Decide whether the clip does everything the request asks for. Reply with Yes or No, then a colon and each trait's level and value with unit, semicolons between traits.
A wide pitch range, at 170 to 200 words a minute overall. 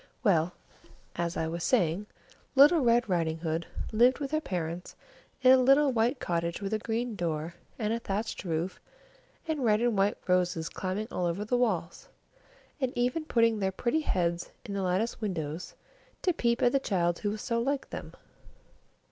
Yes: wide, 5.9 semitones; average, 180 wpm